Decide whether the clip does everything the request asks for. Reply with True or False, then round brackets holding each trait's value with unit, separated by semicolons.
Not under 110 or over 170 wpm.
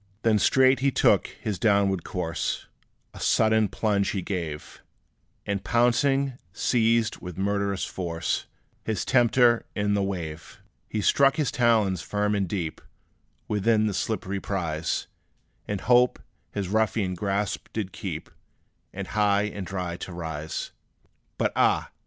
True (135 wpm)